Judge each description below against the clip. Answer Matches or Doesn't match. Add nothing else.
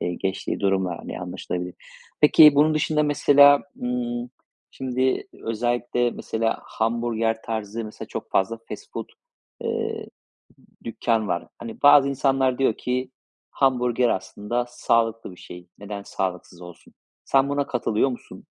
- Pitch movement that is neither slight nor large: Matches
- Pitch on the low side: Matches